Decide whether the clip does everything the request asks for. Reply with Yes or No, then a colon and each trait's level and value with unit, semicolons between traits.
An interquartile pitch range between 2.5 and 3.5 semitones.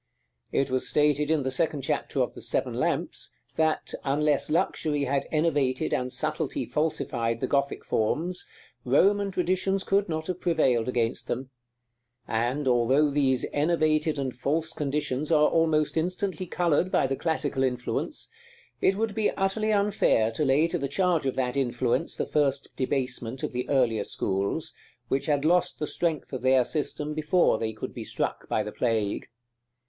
No: average, 4.1 semitones